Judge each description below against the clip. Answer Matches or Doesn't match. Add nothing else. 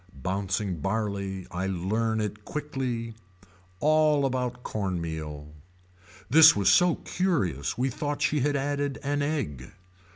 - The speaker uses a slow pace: Matches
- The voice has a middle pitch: Doesn't match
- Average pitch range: Doesn't match